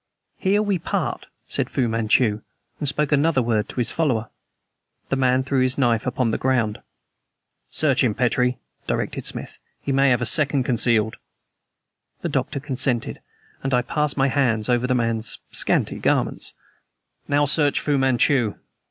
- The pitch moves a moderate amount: Yes, average, 3.1 semitones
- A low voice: Yes, low, 130 Hz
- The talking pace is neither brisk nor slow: Yes, average, 155 wpm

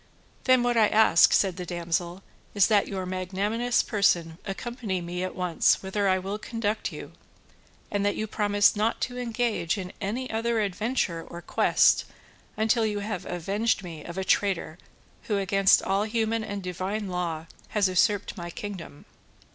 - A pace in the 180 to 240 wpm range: No, average, 165 wpm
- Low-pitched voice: No, high, 200 Hz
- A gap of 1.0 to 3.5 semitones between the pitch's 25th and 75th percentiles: Yes, average, 3.1 semitones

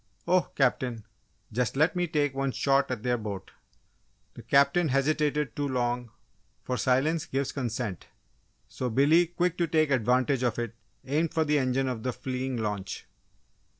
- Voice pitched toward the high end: No, low, 135 Hz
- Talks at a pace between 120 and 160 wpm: Yes, average, 155 wpm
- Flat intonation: No, average, 3.3 semitones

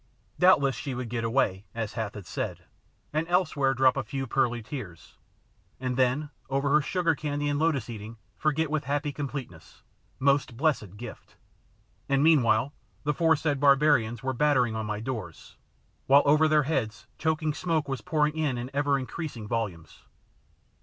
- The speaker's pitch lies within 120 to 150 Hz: Yes, low, 135 Hz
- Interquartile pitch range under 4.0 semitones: No, average, 4.3 semitones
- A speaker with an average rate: Yes, average, 160 wpm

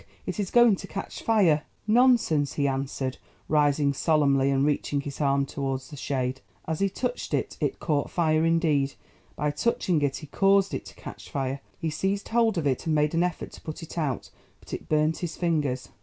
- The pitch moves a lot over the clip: No, average, 4.3 semitones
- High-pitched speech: No, medium, 150 Hz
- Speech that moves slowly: No, average, 200 wpm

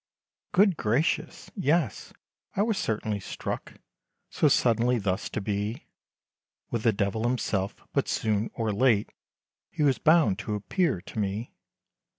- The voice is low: Yes, low, 110 Hz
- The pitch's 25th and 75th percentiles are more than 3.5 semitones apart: Yes, average, 5.2 semitones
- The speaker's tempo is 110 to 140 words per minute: Yes, slow, 135 wpm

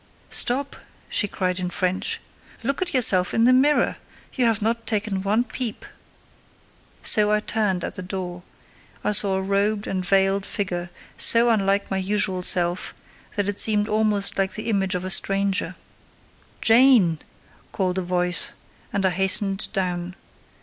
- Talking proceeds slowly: No, average, 150 wpm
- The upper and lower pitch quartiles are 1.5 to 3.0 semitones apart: Yes, narrow, 2.6 semitones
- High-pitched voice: Yes, high, 200 Hz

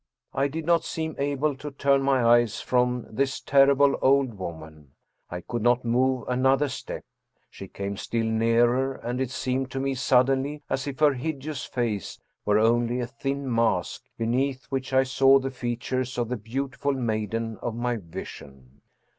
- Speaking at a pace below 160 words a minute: No, average, 165 wpm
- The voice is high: No, low, 125 Hz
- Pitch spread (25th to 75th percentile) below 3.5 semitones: Yes, average, 2.8 semitones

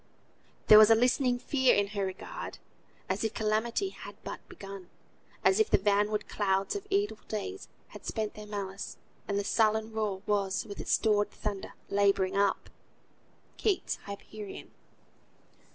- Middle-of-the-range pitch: No, high, 210 Hz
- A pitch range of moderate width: No, narrow, 2.1 semitones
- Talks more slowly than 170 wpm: Yes, average, 150 wpm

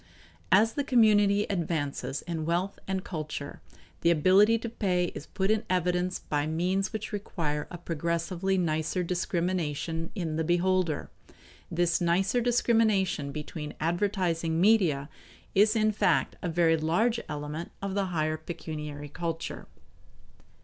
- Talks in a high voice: No, medium, 175 Hz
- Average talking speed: No, slow, 130 wpm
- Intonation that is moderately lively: Yes, average, 3.6 semitones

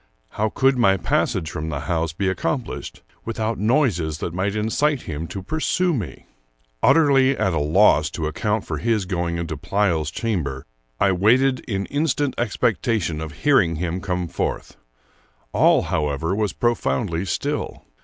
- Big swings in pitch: Yes, wide, 6.1 semitones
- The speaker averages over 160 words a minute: No, average, 150 wpm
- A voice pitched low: Yes, very low, 95 Hz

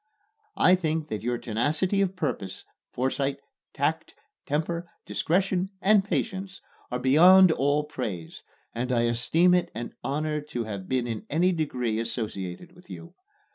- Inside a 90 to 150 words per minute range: Yes, average, 140 wpm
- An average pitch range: No, wide, 6.9 semitones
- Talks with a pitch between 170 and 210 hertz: No, medium, 150 Hz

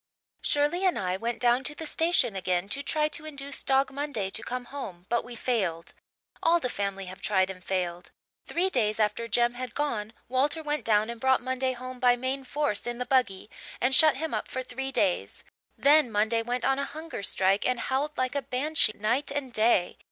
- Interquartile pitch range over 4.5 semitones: Yes, average, 4.9 semitones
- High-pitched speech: Yes, very high, 250 Hz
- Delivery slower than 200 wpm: No, fast, 205 wpm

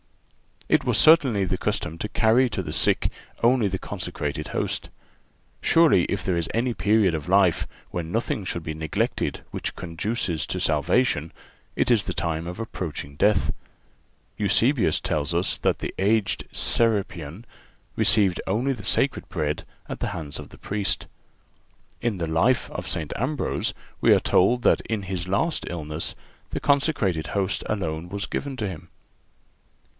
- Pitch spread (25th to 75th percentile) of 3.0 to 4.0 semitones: No, average, 5.3 semitones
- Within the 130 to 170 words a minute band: Yes, average, 155 wpm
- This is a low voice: Yes, very low, 95 Hz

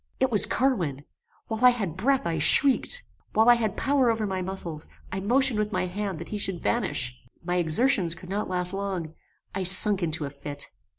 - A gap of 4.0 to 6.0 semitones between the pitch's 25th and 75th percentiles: Yes, average, 5.2 semitones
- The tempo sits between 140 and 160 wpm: No, average, 195 wpm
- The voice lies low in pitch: No, high, 195 Hz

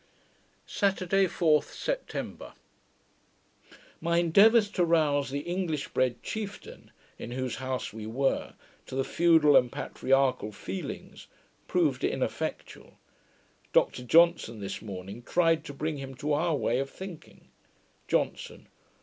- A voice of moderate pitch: Yes, medium, 150 Hz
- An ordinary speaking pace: No, slow, 120 wpm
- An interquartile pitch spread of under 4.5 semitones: No, average, 4.9 semitones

